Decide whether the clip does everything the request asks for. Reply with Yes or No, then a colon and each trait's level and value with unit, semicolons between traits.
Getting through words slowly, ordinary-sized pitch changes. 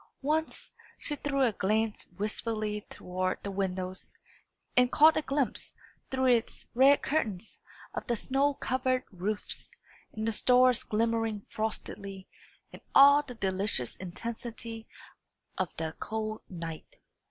Yes: slow, 125 wpm; average, 4.5 semitones